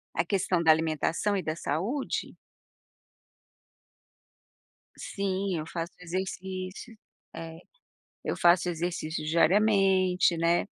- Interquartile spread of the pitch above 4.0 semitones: No, narrow, 2.6 semitones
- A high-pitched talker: No, medium, 180 Hz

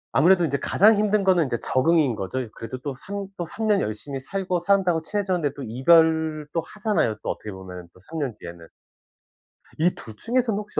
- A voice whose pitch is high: No, medium, 160 Hz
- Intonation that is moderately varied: No, wide, 7.2 semitones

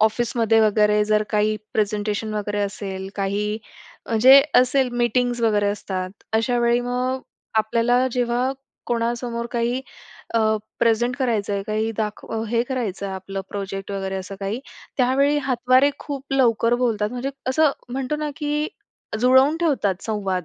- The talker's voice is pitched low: No, high, 230 Hz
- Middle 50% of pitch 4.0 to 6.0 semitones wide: No, average, 3.3 semitones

